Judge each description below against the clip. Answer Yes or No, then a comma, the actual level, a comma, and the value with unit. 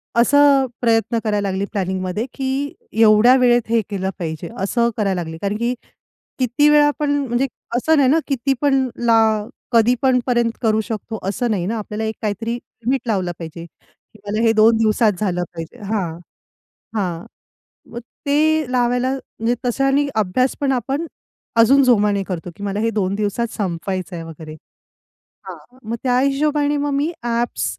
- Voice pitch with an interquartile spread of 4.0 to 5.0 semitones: Yes, average, 4.6 semitones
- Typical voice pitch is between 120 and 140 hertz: No, high, 230 Hz